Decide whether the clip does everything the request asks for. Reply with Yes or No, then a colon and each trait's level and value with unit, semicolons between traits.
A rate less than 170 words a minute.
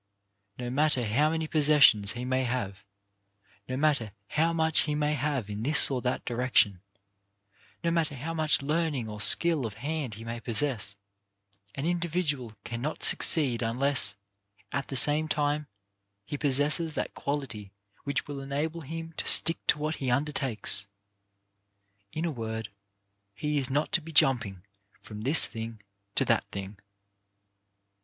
Yes: average, 150 wpm